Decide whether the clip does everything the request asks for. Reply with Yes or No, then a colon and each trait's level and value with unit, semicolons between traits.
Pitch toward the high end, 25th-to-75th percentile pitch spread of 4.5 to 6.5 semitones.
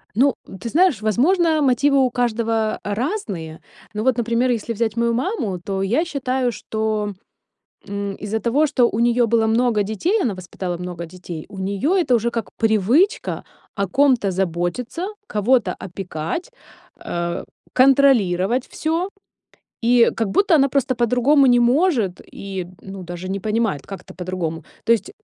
Yes: high, 230 Hz; average, 5.0 semitones